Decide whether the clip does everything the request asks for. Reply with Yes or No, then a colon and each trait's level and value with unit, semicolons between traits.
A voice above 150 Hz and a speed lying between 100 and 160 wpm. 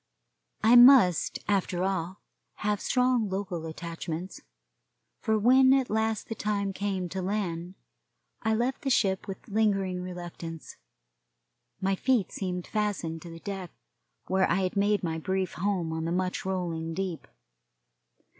Yes: high, 190 Hz; average, 140 wpm